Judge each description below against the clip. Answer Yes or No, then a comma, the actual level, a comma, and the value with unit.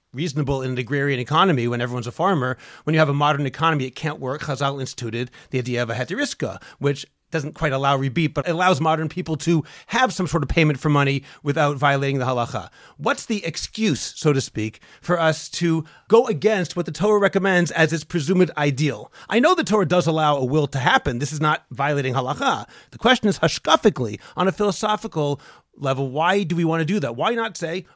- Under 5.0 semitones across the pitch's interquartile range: Yes, average, 4.3 semitones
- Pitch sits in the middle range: Yes, medium, 155 Hz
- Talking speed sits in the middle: No, fast, 215 wpm